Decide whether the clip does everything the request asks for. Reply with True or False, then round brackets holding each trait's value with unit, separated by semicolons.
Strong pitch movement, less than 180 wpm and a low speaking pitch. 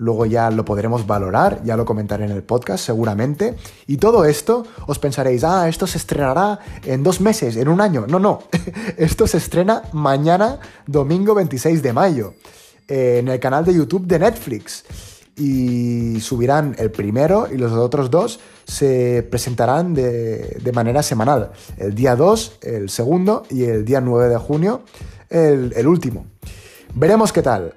True (6.3 semitones; 160 wpm; 130 Hz)